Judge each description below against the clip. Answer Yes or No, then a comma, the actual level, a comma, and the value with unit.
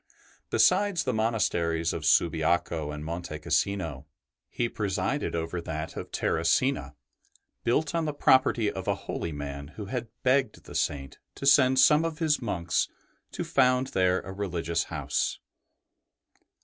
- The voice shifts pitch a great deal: Yes, wide, 7.9 semitones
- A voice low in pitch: Yes, very low, 95 Hz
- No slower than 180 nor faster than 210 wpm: No, average, 140 wpm